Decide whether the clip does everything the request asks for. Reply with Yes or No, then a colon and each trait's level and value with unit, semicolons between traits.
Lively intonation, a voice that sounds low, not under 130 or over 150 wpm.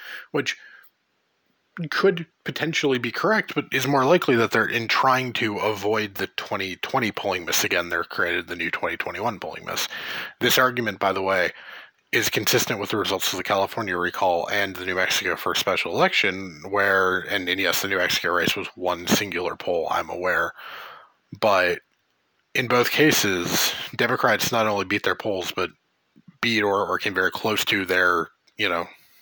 No: wide, 5.9 semitones; low, 115 Hz; average, 175 wpm